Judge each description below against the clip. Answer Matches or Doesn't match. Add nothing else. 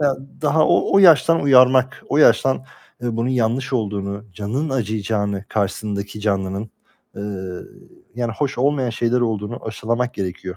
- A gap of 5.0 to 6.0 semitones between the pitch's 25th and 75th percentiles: Doesn't match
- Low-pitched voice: Matches